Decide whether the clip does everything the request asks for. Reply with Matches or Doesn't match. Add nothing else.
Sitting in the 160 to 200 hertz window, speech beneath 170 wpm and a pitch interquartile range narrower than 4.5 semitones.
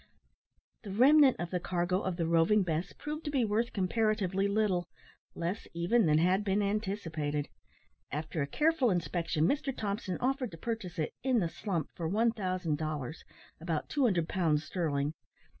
Doesn't match